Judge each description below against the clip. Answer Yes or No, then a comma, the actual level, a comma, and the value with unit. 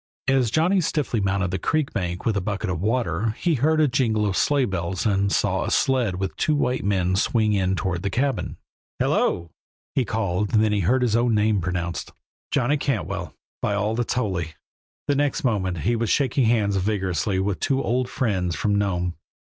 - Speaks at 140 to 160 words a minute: No, average, 185 wpm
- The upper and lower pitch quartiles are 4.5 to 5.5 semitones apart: Yes, average, 5.0 semitones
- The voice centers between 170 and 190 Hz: No, low, 105 Hz